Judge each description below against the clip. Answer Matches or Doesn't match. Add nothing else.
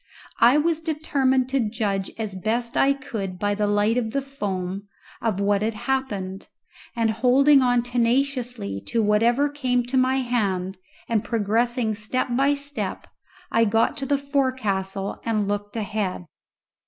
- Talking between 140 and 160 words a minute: Matches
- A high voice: Matches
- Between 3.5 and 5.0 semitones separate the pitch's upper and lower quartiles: Matches